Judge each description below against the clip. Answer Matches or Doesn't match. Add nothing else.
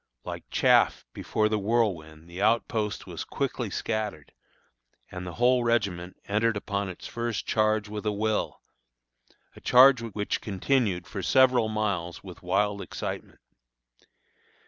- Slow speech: Matches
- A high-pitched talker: Doesn't match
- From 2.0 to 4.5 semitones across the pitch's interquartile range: Matches